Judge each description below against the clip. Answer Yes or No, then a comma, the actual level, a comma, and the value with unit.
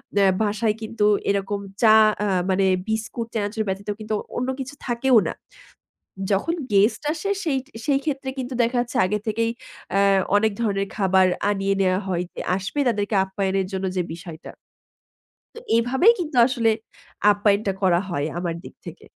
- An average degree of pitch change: Yes, average, 3.5 semitones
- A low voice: No, high, 210 Hz